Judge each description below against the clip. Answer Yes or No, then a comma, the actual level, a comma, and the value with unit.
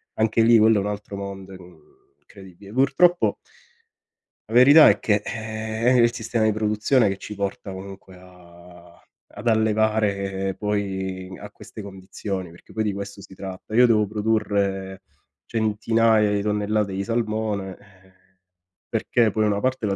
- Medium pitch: No, low, 105 Hz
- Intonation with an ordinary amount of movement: No, narrow, 2.2 semitones